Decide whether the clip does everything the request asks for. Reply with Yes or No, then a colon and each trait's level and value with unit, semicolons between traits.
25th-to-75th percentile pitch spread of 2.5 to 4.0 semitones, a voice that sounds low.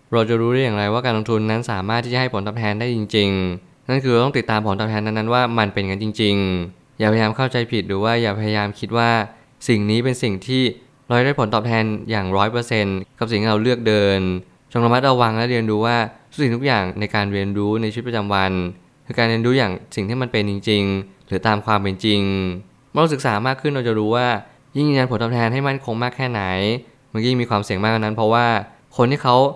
Yes: average, 3.0 semitones; low, 115 Hz